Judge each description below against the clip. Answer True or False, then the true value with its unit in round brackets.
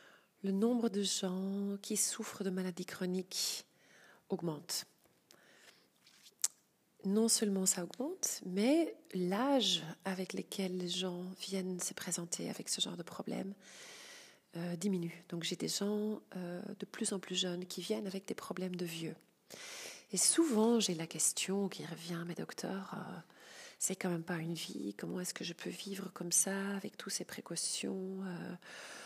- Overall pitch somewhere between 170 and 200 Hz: True (190 Hz)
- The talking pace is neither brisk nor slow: True (160 wpm)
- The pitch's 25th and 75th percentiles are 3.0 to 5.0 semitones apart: False (2.5 semitones)